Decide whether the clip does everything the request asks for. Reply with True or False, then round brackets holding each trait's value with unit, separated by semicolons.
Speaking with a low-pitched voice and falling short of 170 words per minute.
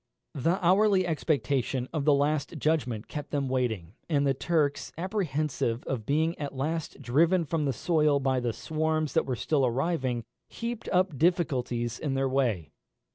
False (145 Hz; 160 wpm)